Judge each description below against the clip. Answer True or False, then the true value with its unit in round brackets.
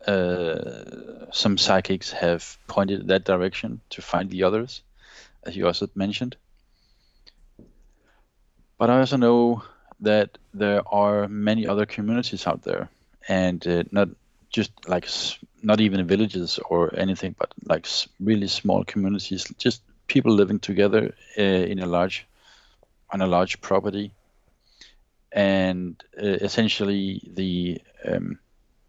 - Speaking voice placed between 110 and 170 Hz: False (100 Hz)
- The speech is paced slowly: True (125 wpm)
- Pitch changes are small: True (2.1 semitones)